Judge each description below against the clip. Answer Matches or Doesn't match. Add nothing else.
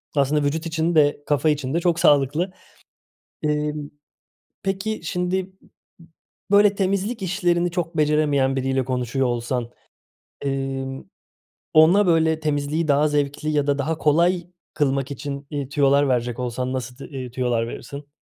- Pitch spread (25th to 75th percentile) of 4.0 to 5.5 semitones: Doesn't match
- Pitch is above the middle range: Doesn't match